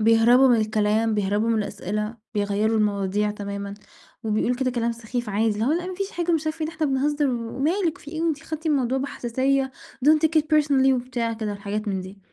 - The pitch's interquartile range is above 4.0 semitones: Yes, wide, 5.5 semitones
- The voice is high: Yes, high, 235 Hz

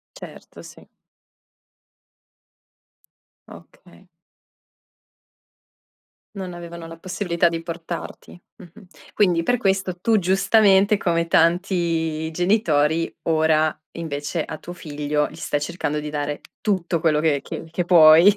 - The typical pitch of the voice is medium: Yes, medium, 170 Hz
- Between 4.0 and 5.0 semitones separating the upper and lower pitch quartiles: No, average, 2.8 semitones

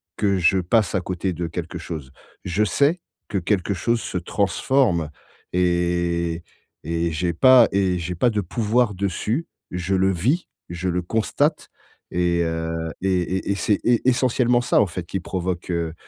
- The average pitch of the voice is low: Yes, very low, 90 Hz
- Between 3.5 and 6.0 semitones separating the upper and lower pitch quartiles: Yes, average, 3.8 semitones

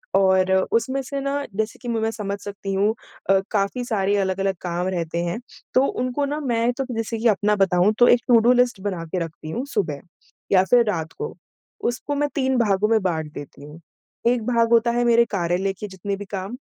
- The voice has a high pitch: Yes, high, 210 Hz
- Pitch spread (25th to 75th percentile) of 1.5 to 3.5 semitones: No, average, 4.3 semitones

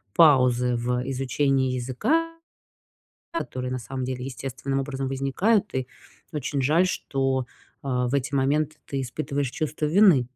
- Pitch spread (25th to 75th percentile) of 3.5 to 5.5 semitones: No, average, 2.7 semitones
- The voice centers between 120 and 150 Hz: Yes, low, 135 Hz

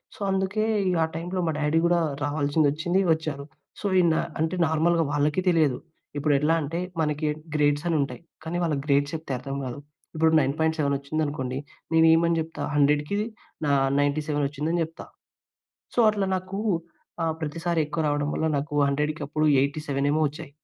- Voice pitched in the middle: Yes, medium, 155 Hz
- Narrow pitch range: Yes, narrow, 2.3 semitones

